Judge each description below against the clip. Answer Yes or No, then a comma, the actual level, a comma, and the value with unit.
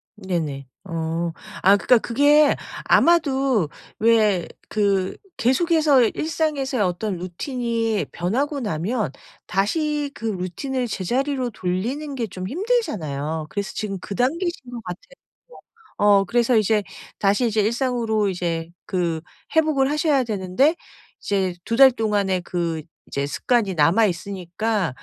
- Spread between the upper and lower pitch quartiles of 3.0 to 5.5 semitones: No, wide, 6.5 semitones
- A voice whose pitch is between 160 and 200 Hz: No, high, 215 Hz